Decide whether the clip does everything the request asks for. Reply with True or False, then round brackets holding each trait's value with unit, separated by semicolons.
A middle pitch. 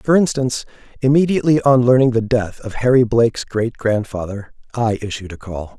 False (120 Hz)